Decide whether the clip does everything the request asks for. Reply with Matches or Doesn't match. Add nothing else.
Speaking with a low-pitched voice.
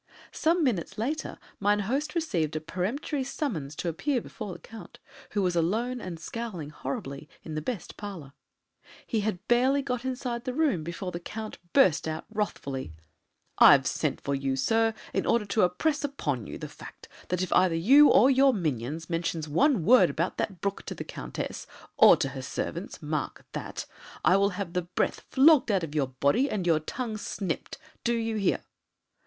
Doesn't match